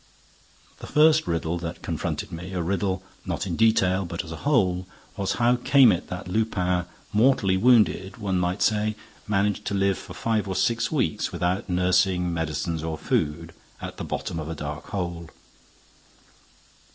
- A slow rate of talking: No, average, 165 wpm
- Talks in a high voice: No, very low, 95 Hz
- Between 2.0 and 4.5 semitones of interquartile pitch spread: Yes, average, 3.7 semitones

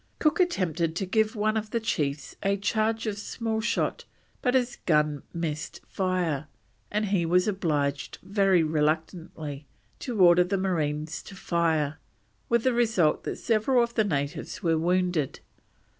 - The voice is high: No, medium, 180 Hz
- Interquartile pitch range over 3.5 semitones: Yes, wide, 5.5 semitones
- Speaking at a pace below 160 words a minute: Yes, average, 150 wpm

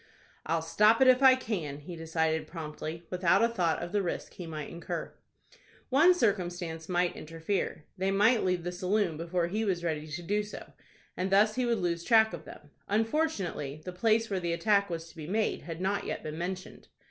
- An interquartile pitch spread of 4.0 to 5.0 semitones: Yes, average, 4.3 semitones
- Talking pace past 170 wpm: Yes, average, 200 wpm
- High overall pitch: No, medium, 180 Hz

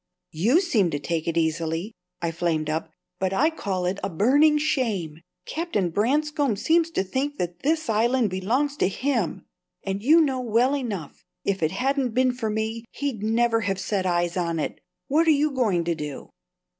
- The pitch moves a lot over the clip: Yes, wide, 7.6 semitones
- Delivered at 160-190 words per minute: Yes, average, 180 wpm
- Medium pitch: No, high, 220 Hz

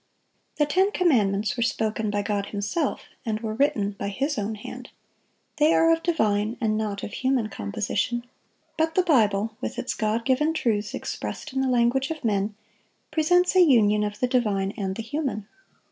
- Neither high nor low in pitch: No, high, 225 Hz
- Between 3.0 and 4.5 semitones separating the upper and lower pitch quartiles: No, wide, 5.5 semitones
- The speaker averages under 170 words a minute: No, average, 175 wpm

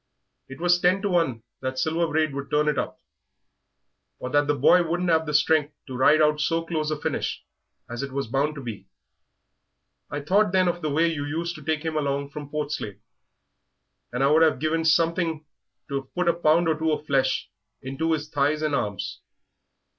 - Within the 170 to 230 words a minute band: Yes, average, 195 wpm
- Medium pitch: Yes, medium, 150 Hz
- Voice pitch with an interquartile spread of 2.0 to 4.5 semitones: Yes, average, 2.8 semitones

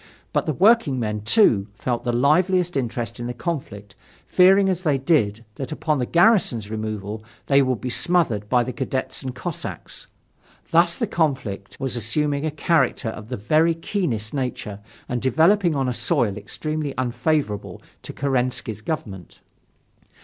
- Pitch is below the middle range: Yes, low, 130 Hz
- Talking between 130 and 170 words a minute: Yes, average, 155 wpm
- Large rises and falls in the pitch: Yes, wide, 6.0 semitones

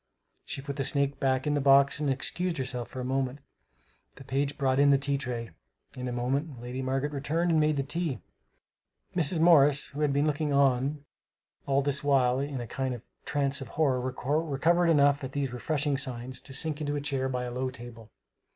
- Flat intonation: Yes, narrow, 2.0 semitones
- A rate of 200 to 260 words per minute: Yes, fast, 205 wpm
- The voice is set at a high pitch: No, medium, 140 Hz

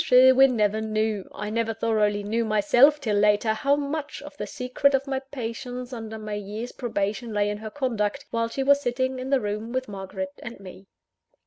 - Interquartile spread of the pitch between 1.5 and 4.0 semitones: Yes, average, 3.7 semitones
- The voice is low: No, high, 225 Hz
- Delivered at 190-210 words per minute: Yes, average, 195 wpm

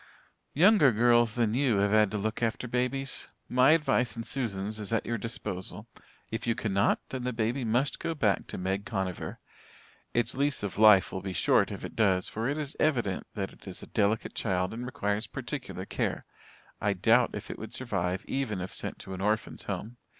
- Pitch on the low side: Yes, low, 110 Hz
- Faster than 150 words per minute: Yes, average, 200 wpm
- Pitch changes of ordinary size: Yes, average, 3.9 semitones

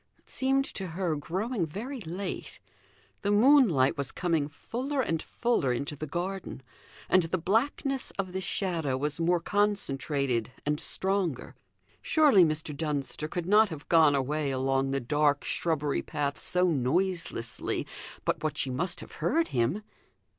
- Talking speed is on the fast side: No, average, 145 wpm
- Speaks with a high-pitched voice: No, medium, 165 Hz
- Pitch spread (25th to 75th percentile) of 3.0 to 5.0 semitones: No, wide, 5.5 semitones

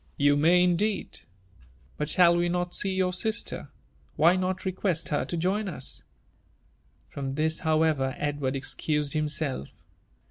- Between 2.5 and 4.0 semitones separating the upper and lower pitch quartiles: Yes, average, 3.7 semitones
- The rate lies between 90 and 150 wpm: Yes, average, 140 wpm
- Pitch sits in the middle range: Yes, medium, 165 Hz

